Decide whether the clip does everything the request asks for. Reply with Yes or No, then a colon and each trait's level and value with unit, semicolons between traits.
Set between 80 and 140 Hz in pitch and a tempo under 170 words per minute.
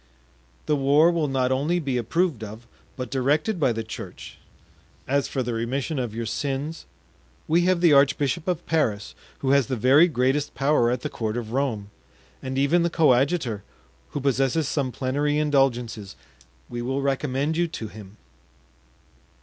Yes: low, 135 Hz; average, 160 wpm